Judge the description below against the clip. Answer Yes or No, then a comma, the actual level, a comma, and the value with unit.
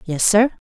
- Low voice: No, high, 195 Hz